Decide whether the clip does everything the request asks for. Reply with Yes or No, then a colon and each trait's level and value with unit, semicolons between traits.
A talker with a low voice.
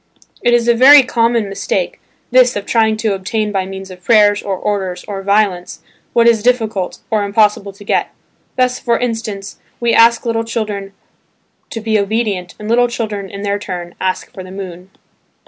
No: high, 210 Hz